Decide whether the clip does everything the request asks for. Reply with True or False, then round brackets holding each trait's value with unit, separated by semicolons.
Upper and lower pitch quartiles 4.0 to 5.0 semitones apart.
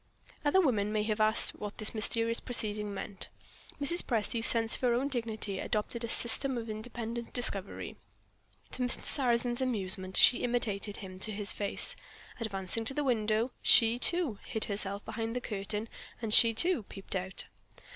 False (2.6 semitones)